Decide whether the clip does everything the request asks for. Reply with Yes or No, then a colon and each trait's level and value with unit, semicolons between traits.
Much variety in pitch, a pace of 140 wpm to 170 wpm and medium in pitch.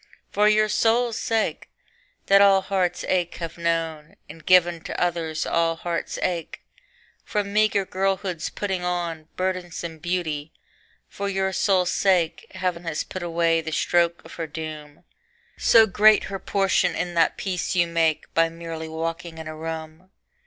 No: average, 2.7 semitones; average, 150 wpm; medium, 175 Hz